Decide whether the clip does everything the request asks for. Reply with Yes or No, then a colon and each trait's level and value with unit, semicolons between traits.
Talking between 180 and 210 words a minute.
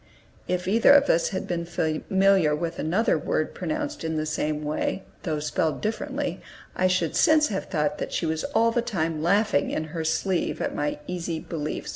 Yes: average, 185 wpm